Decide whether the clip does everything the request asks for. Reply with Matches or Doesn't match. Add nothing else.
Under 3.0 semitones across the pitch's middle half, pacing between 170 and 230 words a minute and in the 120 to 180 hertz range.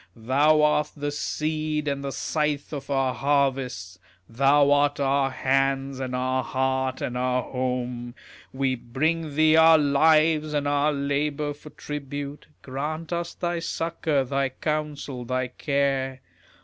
Doesn't match